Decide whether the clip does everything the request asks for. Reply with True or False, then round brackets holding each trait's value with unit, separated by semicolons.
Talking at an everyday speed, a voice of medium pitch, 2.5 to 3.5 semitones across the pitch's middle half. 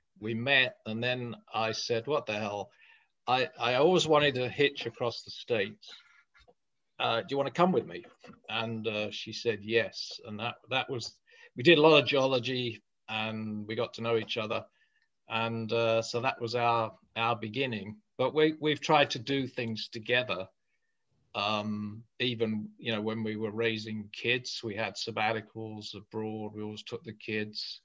False (175 wpm; 115 Hz; 2.9 semitones)